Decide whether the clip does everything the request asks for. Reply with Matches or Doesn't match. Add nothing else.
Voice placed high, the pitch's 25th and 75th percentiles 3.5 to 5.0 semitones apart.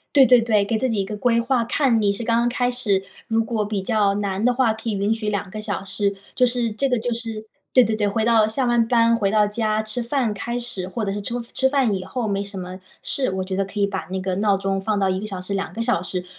Doesn't match